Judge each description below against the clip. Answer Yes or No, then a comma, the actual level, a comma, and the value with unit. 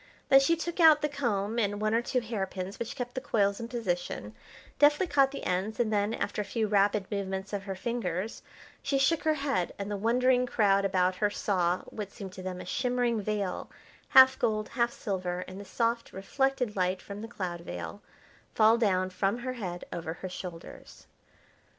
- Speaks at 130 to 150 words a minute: No, average, 195 wpm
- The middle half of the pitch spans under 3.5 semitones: No, average, 4.4 semitones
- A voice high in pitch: Yes, high, 210 Hz